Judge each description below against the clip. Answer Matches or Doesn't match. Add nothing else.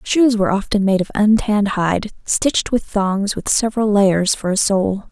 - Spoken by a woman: Matches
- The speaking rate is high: Doesn't match